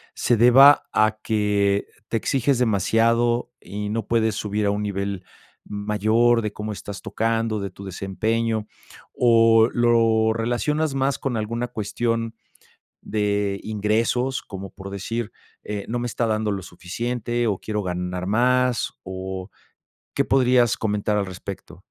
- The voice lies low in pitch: Yes, low, 110 Hz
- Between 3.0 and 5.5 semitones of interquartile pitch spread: No, narrow, 2.6 semitones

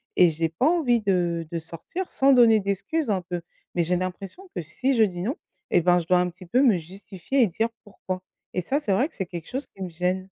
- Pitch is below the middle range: No, high, 190 Hz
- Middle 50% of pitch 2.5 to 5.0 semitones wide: No, wide, 5.4 semitones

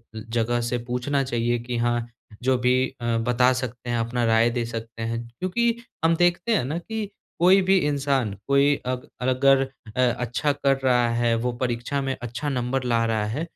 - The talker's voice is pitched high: No, low, 125 Hz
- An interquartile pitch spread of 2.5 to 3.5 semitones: Yes, average, 2.9 semitones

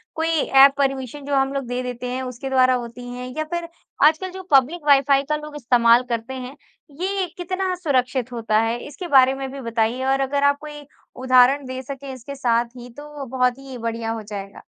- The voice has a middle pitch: No, very high, 265 Hz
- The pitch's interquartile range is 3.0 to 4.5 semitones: No, narrow, 2.6 semitones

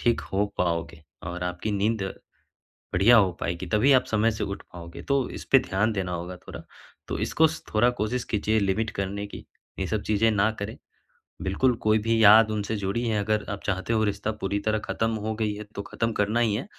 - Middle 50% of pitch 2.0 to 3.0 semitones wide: Yes, narrow, 2.5 semitones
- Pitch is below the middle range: Yes, low, 105 Hz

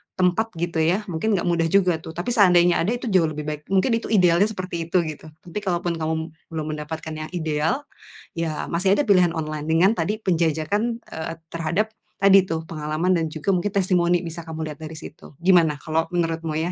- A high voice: No, medium, 170 Hz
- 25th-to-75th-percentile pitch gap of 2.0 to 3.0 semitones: Yes, average, 2.7 semitones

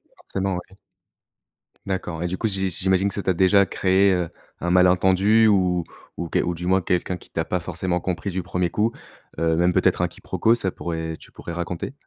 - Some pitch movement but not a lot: No, narrow, 1.7 semitones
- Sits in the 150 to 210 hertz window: No, very low, 90 Hz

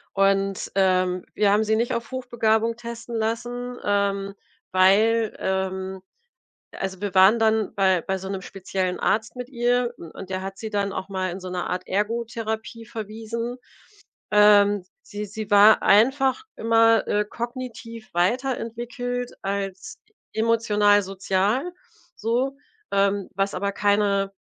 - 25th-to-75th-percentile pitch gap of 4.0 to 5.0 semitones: No, average, 2.9 semitones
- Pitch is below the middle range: No, high, 210 Hz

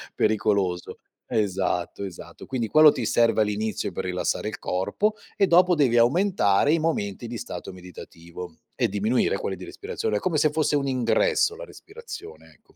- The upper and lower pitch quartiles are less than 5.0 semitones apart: No, wide, 8.1 semitones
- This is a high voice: No, low, 115 Hz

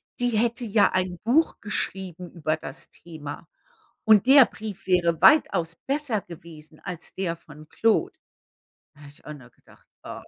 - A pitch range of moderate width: No, wide, 5.8 semitones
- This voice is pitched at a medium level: Yes, medium, 180 Hz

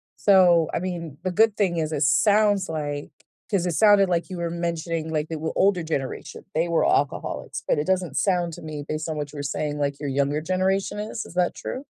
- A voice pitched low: No, medium, 170 Hz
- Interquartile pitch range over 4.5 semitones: No, average, 3.6 semitones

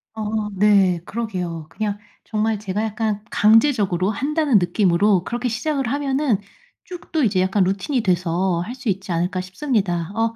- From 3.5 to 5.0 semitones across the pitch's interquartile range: Yes, average, 4.1 semitones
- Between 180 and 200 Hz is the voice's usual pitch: No, high, 210 Hz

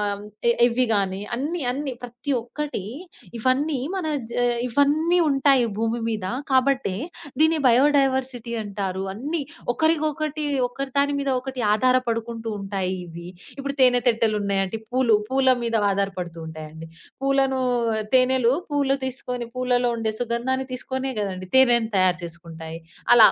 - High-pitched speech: Yes, high, 245 Hz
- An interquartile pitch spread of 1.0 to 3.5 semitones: No, average, 4.3 semitones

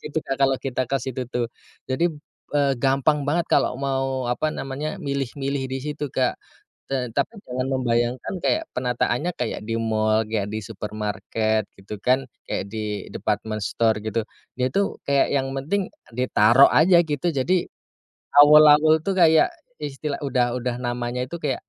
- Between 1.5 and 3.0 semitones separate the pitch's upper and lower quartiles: No, average, 3.8 semitones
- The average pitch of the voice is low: Yes, low, 130 Hz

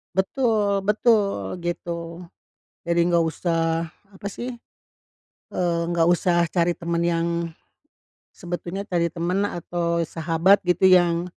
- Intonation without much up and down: Yes, narrow, 2.2 semitones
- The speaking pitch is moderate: Yes, medium, 175 Hz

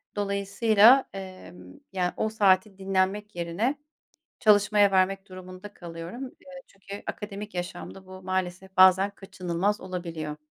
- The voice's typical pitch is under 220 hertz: Yes, high, 190 Hz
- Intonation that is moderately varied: No, narrow, 2.0 semitones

